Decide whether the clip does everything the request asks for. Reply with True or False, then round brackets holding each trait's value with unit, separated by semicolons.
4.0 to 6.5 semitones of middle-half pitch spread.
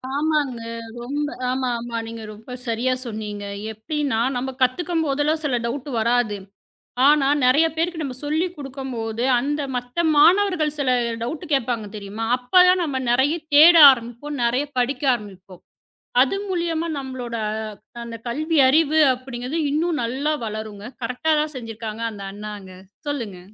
True (4.6 semitones)